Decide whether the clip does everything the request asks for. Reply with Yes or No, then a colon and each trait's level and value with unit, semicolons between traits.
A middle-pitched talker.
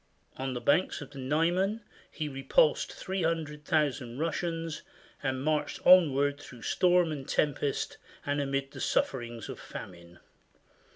Yes: medium, 145 Hz